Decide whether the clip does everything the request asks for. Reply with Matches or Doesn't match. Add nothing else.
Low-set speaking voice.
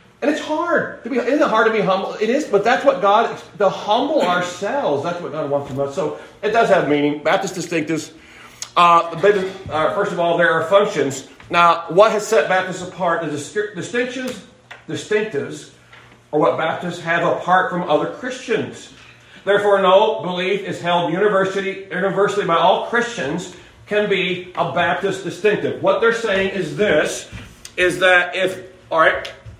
Doesn't match